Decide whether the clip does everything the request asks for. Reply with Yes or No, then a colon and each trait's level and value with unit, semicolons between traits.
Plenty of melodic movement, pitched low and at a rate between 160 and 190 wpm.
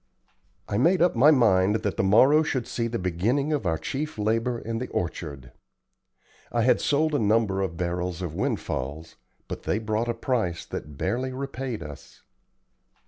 Yes: wide, 6.1 semitones; low, 110 Hz; average, 170 wpm